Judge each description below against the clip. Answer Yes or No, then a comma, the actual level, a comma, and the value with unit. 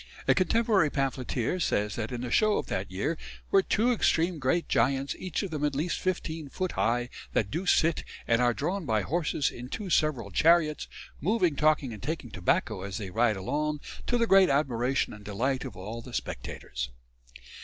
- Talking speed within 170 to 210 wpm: Yes, average, 185 wpm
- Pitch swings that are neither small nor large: No, wide, 6.6 semitones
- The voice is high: No, medium, 140 Hz